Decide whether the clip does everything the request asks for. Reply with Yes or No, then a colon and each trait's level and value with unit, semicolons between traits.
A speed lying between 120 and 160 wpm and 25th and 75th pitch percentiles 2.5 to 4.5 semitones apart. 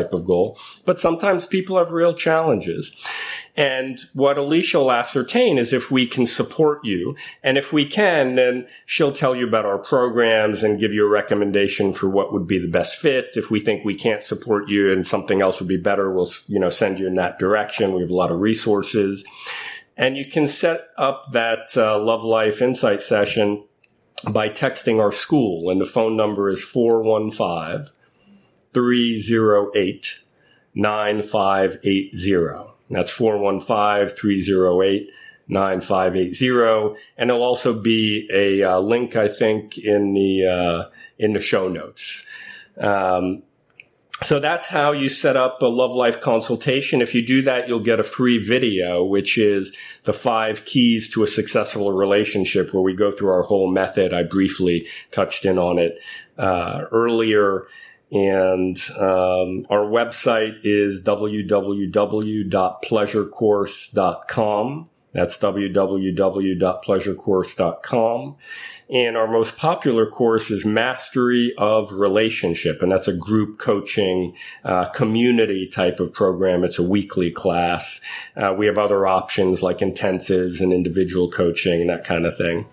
Yes: average, 145 wpm; average, 4.2 semitones